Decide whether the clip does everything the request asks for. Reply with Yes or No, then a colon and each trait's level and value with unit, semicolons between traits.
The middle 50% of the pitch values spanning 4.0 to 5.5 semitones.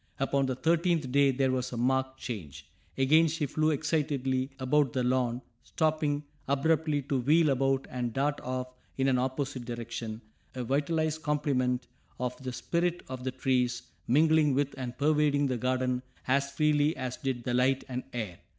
No: average, 2.7 semitones